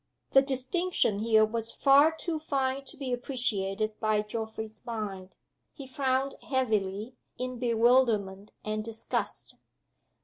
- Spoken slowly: Yes, slow, 115 wpm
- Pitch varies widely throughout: No, average, 3.7 semitones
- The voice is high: Yes, high, 235 Hz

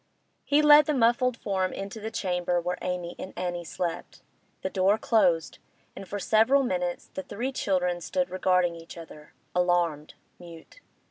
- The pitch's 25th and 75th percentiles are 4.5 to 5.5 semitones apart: No, average, 4.1 semitones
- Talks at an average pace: Yes, average, 155 wpm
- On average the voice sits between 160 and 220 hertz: Yes, medium, 185 Hz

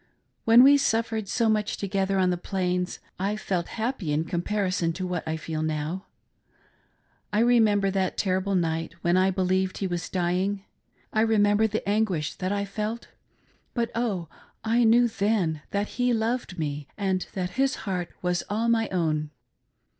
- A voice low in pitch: No, high, 195 Hz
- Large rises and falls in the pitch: No, average, 3.7 semitones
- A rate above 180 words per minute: No, average, 165 wpm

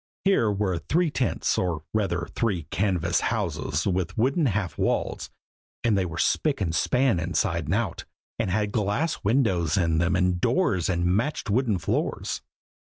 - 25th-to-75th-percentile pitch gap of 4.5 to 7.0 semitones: Yes, average, 4.9 semitones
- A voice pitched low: Yes, very low, 95 Hz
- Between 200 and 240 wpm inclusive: No, average, 160 wpm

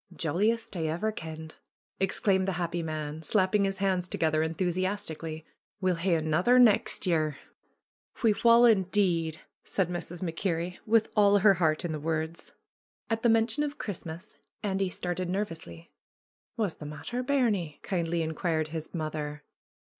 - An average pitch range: Yes, average, 4.2 semitones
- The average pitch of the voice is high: No, medium, 175 Hz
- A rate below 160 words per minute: Yes, average, 145 wpm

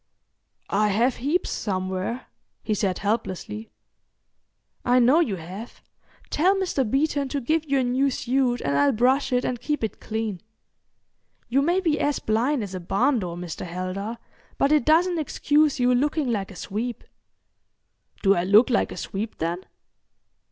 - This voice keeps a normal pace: Yes, average, 160 wpm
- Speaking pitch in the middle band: No, high, 240 Hz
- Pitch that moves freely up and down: Yes, wide, 5.9 semitones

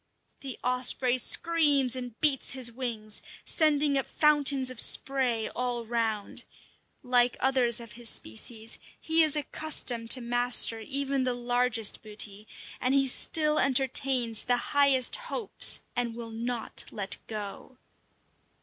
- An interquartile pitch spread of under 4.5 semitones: Yes, average, 2.8 semitones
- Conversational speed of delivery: No, slow, 130 wpm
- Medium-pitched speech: No, very high, 250 Hz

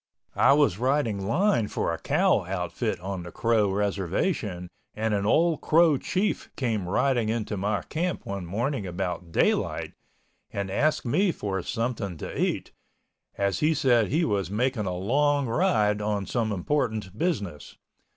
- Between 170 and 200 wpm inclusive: No, average, 150 wpm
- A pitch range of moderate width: No, wide, 6.1 semitones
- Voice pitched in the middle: No, low, 110 Hz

